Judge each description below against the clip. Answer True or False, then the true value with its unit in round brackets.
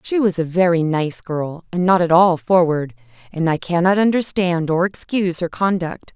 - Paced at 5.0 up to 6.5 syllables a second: False (4.8 syllables/s)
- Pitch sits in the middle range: True (170 Hz)